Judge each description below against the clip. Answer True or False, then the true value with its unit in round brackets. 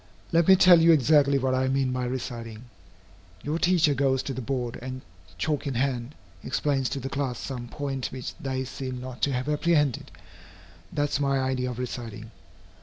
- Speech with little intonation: True (2.3 semitones)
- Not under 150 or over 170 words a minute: False (180 wpm)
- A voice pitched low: True (130 Hz)